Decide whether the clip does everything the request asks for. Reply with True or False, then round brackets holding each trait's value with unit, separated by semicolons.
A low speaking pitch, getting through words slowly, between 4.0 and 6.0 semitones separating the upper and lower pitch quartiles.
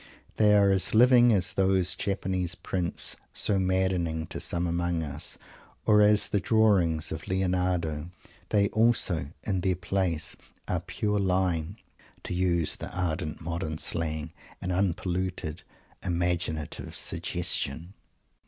False (90 Hz; 125 wpm; 2.5 semitones)